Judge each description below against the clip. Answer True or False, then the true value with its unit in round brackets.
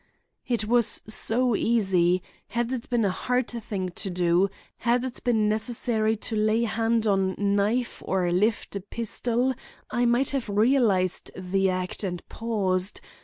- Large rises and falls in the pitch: False (3.7 semitones)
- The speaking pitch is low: False (215 Hz)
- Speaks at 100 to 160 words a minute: True (150 wpm)